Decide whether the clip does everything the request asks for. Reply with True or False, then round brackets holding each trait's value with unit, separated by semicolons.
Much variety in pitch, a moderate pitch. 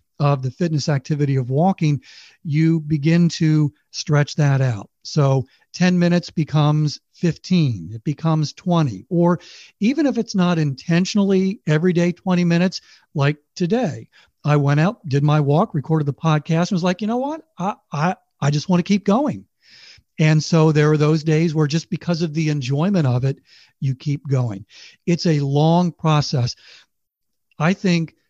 False (3.4 semitones; 160 Hz)